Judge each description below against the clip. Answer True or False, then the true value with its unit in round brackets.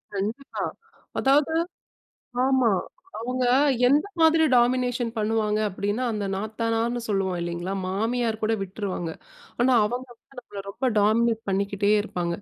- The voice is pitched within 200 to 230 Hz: True (225 Hz)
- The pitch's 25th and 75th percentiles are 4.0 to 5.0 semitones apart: False (3.6 semitones)